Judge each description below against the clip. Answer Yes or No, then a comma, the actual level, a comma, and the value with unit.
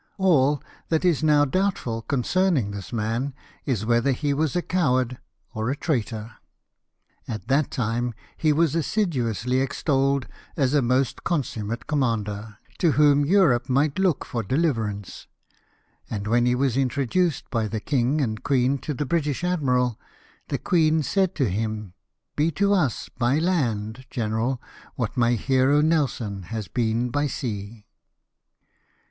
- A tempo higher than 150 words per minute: No, average, 145 wpm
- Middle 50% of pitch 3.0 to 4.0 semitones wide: No, average, 4.8 semitones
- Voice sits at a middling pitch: No, low, 130 Hz